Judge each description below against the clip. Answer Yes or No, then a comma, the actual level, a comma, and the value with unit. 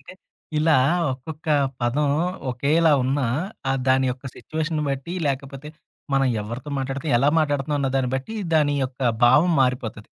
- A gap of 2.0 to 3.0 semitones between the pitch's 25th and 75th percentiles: Yes, narrow, 2.6 semitones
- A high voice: No, low, 135 Hz